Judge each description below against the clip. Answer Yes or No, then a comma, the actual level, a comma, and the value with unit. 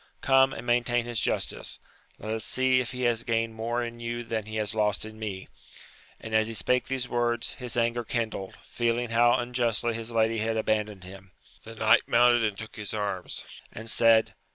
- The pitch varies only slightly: Yes, narrow, 1.6 semitones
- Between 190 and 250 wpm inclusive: Yes, average, 195 wpm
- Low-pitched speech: Yes, low, 115 Hz